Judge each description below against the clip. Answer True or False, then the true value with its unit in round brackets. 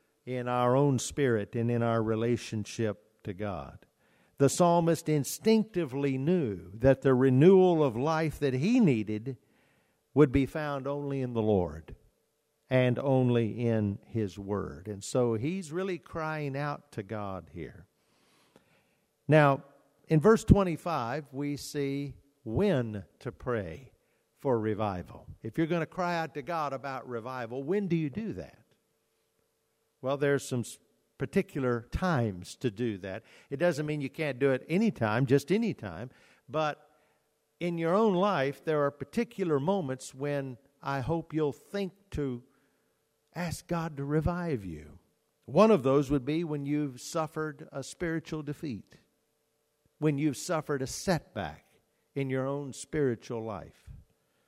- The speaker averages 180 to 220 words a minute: False (140 wpm)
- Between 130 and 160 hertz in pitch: True (140 Hz)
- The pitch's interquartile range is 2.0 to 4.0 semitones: False (4.7 semitones)